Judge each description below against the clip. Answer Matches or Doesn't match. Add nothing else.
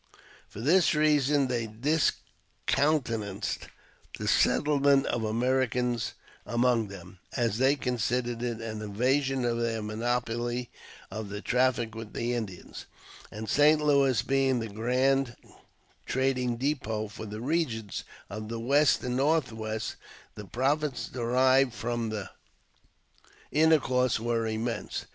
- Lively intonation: Doesn't match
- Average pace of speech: Doesn't match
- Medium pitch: Doesn't match